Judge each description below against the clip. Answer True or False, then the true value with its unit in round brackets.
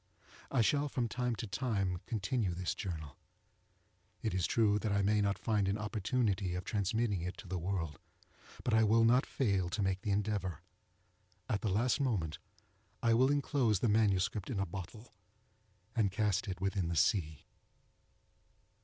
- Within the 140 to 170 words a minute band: True (165 wpm)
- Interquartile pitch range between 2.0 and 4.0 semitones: True (3.5 semitones)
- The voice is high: False (100 Hz)